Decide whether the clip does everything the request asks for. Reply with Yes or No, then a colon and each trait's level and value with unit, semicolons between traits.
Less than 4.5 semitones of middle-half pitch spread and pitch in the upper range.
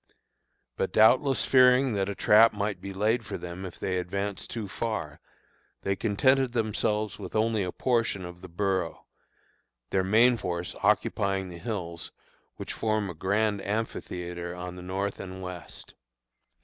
No: average, 3.5 semitones; low, 100 Hz